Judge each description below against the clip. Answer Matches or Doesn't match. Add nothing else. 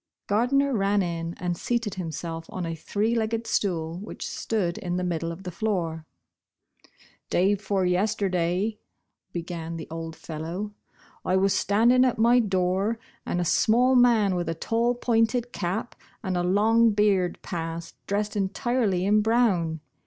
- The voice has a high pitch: Matches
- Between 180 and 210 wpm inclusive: Doesn't match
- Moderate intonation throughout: Matches